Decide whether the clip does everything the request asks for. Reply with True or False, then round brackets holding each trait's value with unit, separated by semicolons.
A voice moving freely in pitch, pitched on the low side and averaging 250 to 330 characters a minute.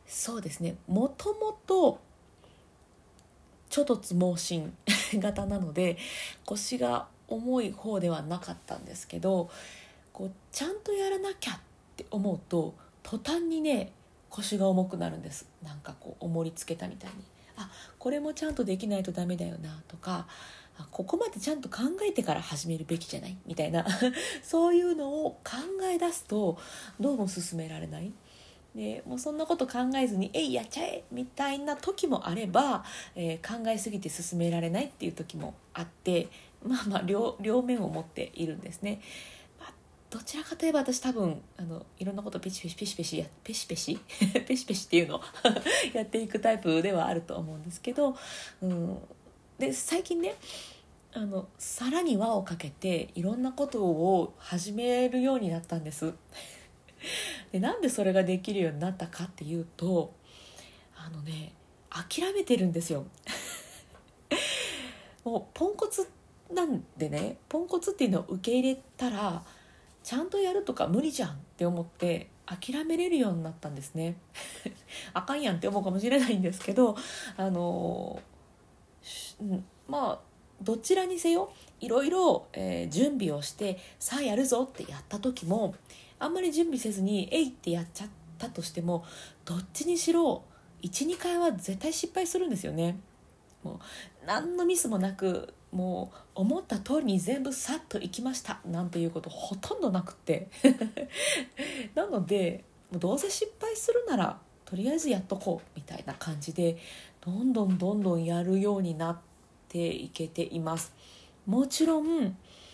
False (7.7 semitones; 200 Hz; 315 characters per minute)